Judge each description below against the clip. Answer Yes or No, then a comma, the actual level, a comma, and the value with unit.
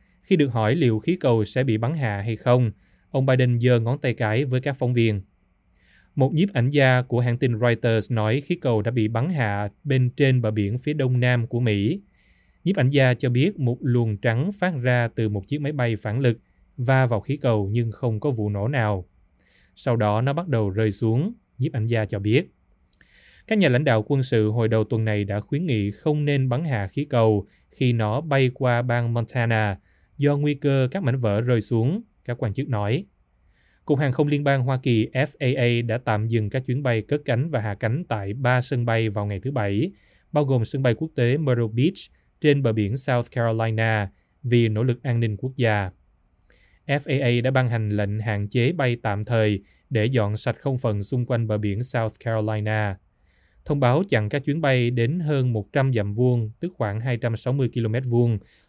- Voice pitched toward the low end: Yes, low, 120 Hz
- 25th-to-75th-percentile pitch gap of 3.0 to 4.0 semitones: Yes, average, 3.5 semitones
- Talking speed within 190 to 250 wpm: Yes, average, 210 wpm